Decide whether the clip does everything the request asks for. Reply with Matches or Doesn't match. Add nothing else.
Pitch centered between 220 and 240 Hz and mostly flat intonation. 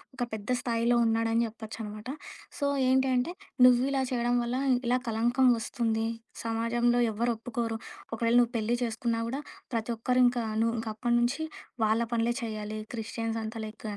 Matches